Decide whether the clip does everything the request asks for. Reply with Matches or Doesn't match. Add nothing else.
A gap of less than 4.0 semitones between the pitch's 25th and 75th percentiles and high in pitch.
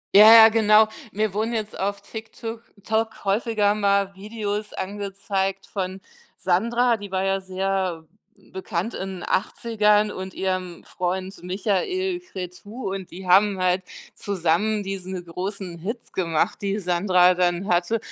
Matches